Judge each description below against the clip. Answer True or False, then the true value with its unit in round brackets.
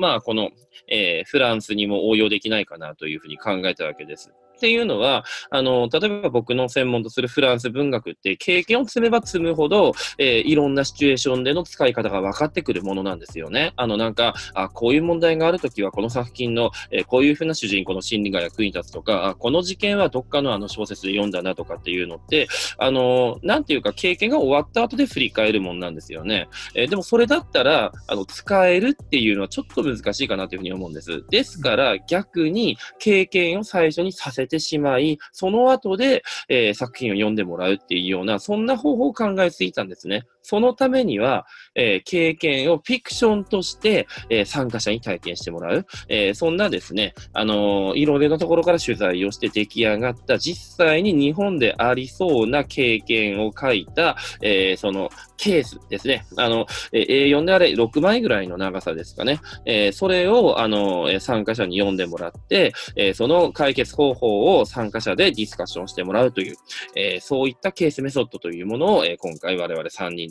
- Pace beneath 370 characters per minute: False (420 characters per minute)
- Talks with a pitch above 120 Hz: True (130 Hz)